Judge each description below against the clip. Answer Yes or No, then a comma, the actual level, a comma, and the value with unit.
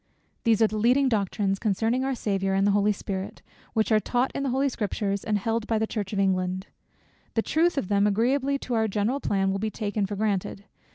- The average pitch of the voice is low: No, high, 215 Hz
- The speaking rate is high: Yes, fast, 220 wpm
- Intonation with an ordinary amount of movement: Yes, average, 3.1 semitones